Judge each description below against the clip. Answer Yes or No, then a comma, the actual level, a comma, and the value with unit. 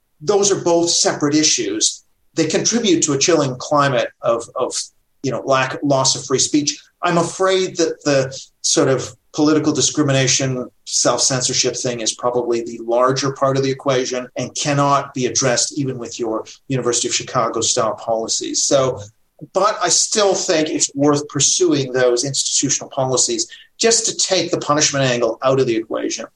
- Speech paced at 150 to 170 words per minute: Yes, average, 165 wpm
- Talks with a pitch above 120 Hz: Yes, medium, 140 Hz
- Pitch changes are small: No, average, 5.3 semitones